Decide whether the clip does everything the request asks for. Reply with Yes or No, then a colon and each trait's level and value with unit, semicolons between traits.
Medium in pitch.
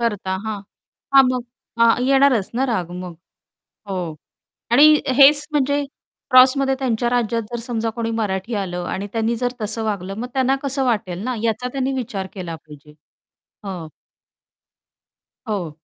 No: high, 230 Hz